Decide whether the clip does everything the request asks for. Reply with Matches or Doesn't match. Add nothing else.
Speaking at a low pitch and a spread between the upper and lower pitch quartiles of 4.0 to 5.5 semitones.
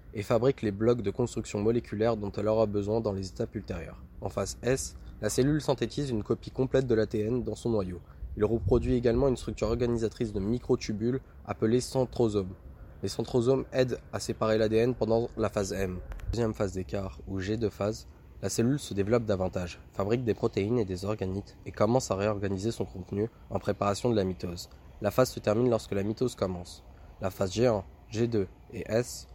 Doesn't match